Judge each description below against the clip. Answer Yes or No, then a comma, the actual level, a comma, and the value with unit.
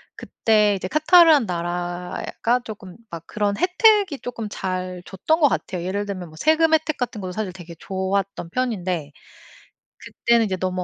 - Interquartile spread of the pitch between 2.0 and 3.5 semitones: No, wide, 5.6 semitones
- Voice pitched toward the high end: Yes, high, 200 Hz